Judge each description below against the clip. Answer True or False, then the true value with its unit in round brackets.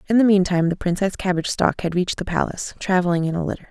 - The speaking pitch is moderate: True (180 Hz)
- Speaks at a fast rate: True (245 wpm)